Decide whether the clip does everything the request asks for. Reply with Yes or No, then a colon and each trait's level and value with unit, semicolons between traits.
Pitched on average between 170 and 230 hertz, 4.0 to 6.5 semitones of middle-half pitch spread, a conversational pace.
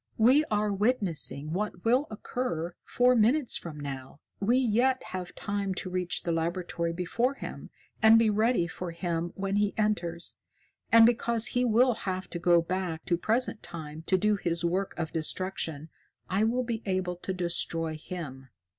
Yes: medium, 185 Hz; average, 4.8 semitones; average, 165 wpm